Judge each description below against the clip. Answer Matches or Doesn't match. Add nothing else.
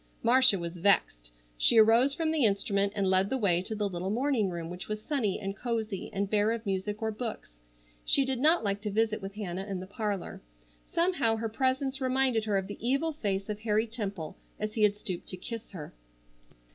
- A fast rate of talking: Matches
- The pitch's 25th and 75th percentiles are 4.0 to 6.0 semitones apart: Doesn't match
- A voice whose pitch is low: Doesn't match